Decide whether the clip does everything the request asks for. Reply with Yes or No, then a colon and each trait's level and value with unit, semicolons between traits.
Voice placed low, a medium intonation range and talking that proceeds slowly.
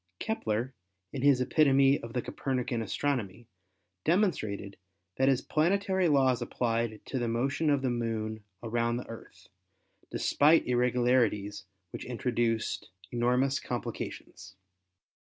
Yes: low, 125 Hz; average, 3.0 semitones; slow, 115 wpm